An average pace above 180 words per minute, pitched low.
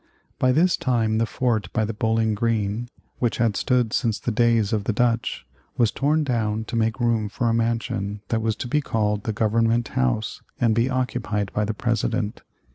Yes: average, 195 wpm; low, 115 Hz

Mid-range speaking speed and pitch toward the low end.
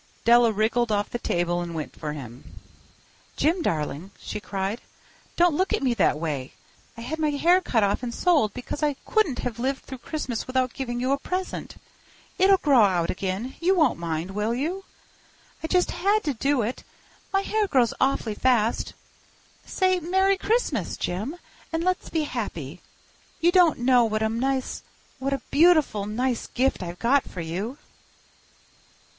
No: average, 165 wpm; very high, 250 Hz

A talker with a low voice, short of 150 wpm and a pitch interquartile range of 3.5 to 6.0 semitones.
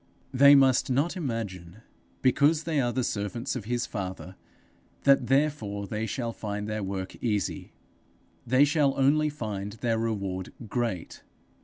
Yes: low, 115 Hz; average, 140 wpm; average, 5.1 semitones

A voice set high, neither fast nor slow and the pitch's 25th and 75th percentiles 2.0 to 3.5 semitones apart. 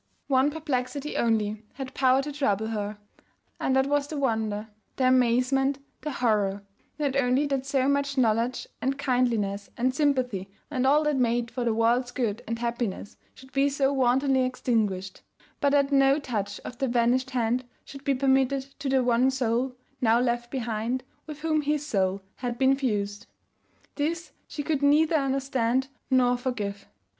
Yes: very high, 255 Hz; average, 165 wpm; average, 3.0 semitones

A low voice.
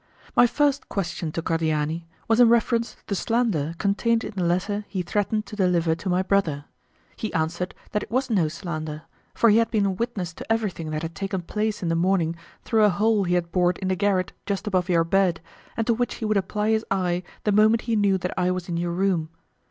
No: high, 190 Hz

